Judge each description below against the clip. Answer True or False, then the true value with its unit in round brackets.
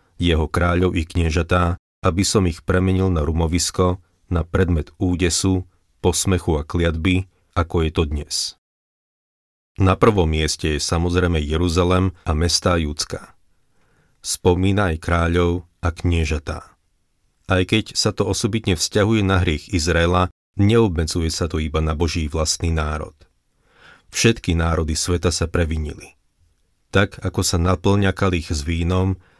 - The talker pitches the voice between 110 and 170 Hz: False (90 Hz)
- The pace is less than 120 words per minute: False (130 wpm)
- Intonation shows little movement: True (2.2 semitones)